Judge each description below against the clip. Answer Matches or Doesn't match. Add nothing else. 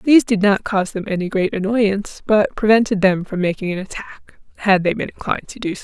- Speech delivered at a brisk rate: Matches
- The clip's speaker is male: Doesn't match